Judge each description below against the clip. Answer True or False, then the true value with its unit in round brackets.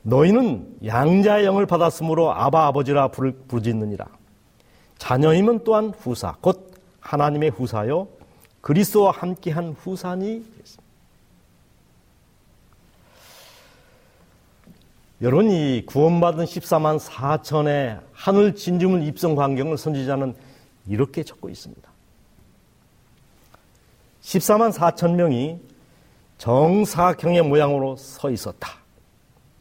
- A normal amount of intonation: True (5.0 semitones)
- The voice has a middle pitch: True (155 Hz)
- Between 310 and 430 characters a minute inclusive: False (215 characters per minute)